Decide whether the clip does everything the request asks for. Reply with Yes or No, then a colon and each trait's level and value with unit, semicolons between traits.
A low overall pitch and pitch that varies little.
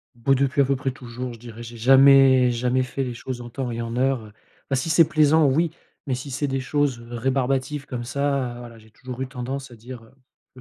Yes: low, 130 Hz; narrow, 2.2 semitones